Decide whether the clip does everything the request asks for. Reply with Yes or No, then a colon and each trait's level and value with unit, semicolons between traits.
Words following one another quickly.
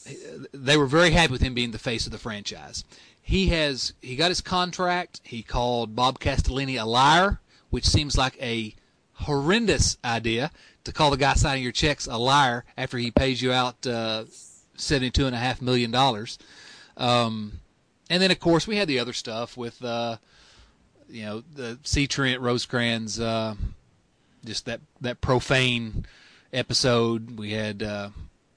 No: average, 165 wpm